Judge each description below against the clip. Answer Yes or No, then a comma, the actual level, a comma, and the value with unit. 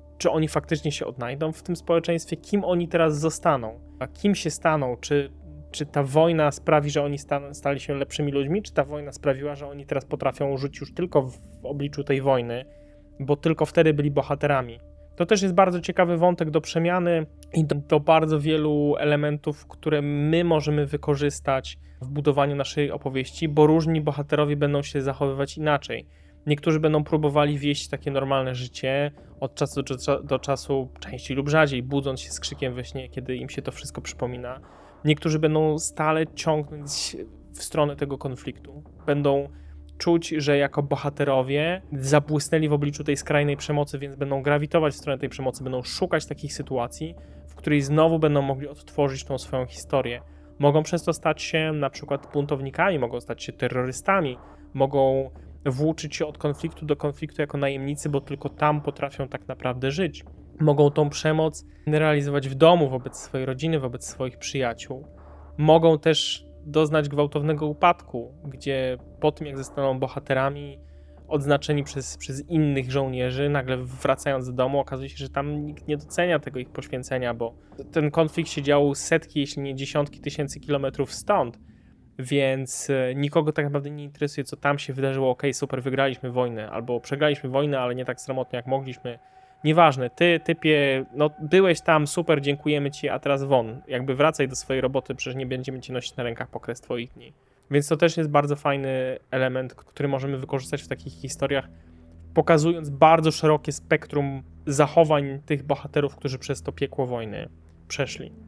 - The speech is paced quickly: Yes, fast, 165 wpm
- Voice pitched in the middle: Yes, medium, 145 Hz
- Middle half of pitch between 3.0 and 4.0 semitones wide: No, narrow, 2.4 semitones